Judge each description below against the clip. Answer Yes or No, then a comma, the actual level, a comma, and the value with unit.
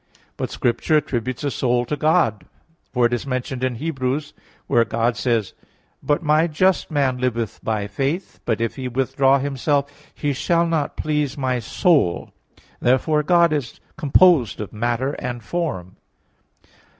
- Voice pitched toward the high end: No, low, 130 Hz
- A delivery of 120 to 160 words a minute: Yes, average, 155 wpm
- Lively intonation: No, average, 4.0 semitones